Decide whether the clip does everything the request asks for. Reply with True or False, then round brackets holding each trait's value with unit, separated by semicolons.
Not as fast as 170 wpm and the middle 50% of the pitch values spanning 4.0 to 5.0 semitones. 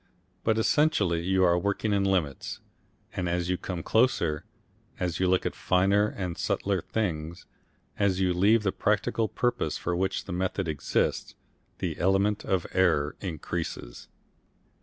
False (145 wpm; 2.7 semitones)